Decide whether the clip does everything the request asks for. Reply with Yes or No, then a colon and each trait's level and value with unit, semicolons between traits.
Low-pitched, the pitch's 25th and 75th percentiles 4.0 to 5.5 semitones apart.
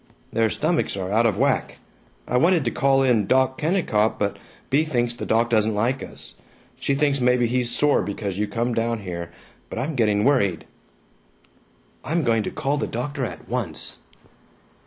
Yes: low, 120 Hz; average, 4.3 semitones